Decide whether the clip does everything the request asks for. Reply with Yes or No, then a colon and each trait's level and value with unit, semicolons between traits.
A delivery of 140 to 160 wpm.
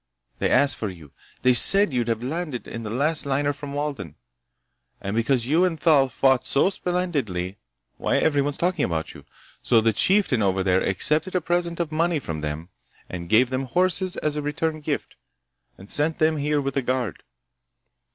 No: average, 180 wpm